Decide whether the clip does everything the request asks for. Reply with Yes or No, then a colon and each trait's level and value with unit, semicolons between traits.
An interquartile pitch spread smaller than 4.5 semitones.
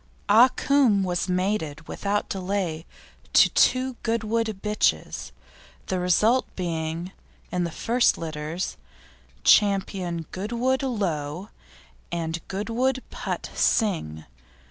No: wide, 5.4 semitones